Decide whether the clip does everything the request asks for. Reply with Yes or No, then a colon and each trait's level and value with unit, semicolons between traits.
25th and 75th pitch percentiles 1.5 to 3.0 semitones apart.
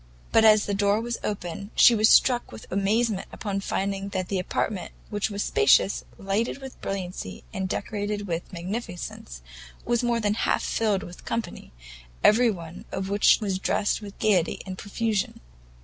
Yes: narrow, 2.5 semitones